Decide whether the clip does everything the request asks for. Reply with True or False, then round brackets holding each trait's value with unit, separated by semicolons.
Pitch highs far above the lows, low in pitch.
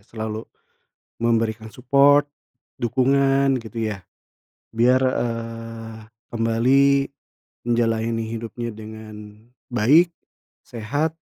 False (3.2 semitones; 115 Hz)